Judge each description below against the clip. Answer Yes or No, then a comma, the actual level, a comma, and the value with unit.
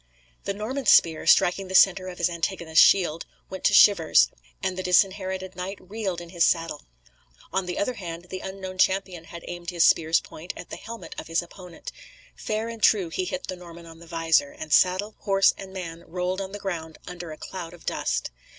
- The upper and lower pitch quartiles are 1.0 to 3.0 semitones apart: Yes, narrow, 2.4 semitones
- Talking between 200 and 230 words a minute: Yes, fast, 205 wpm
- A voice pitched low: No, medium, 180 Hz